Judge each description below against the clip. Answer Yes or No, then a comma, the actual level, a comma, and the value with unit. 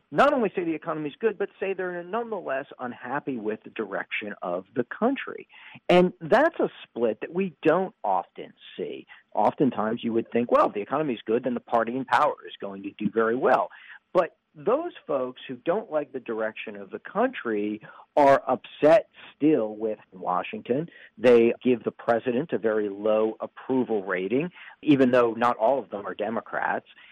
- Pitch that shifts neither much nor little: No, wide, 8.9 semitones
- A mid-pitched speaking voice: No, low, 130 Hz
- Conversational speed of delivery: Yes, average, 180 wpm